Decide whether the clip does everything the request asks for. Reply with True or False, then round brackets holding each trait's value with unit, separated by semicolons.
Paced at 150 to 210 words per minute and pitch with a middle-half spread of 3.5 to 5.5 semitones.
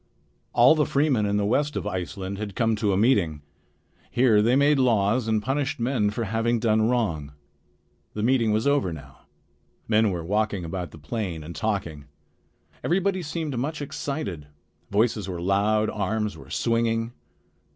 True (160 wpm; 4.1 semitones)